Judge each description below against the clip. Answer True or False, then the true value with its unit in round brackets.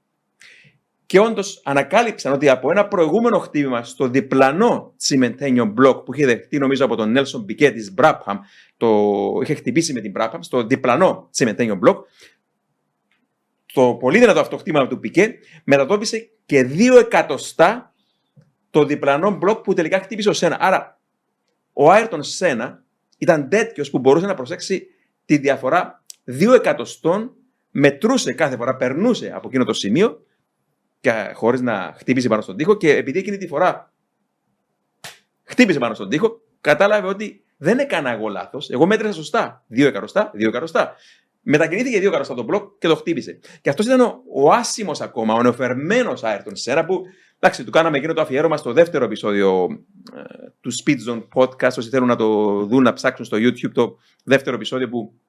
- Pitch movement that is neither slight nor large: False (8.5 semitones)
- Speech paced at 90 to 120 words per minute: False (160 wpm)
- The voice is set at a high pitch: False (150 Hz)